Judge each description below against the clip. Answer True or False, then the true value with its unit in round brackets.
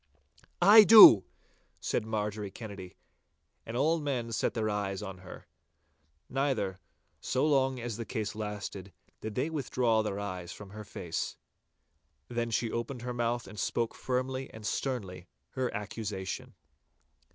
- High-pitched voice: False (110 Hz)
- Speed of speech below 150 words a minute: True (140 wpm)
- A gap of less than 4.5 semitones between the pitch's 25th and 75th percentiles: True (3.9 semitones)